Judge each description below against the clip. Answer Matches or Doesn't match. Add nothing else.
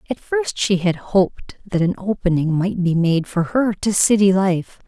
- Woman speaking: Matches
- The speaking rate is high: Doesn't match